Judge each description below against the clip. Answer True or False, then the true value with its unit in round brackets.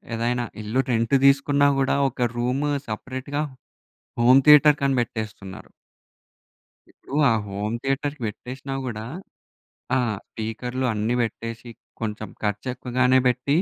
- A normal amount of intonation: True (3.3 semitones)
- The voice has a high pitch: False (125 Hz)